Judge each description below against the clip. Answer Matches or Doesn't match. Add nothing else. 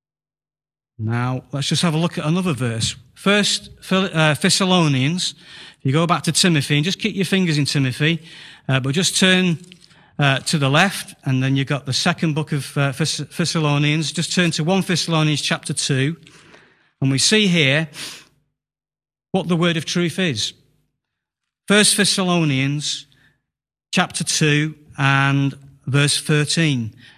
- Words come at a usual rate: Matches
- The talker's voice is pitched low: Doesn't match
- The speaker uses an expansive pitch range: Doesn't match